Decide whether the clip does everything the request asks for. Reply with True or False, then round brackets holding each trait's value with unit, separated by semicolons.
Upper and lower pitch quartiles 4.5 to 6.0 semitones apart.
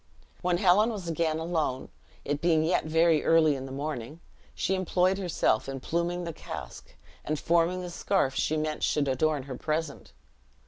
False (3.3 semitones)